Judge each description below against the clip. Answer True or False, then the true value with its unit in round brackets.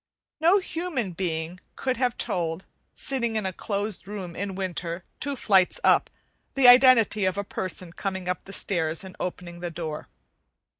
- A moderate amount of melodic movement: True (5.0 semitones)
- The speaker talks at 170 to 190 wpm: False (160 wpm)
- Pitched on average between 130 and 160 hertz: False (190 Hz)